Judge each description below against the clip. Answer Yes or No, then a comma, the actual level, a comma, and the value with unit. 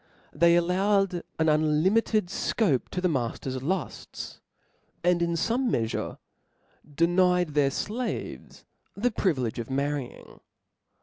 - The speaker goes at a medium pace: No, slow, 115 wpm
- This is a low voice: No, medium, 170 Hz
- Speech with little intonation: No, average, 4.8 semitones